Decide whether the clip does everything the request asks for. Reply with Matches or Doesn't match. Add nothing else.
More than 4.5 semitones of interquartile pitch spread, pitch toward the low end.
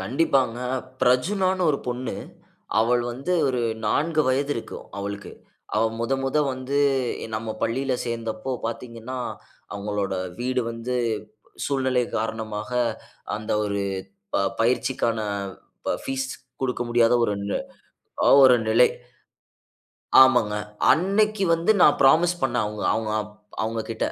Doesn't match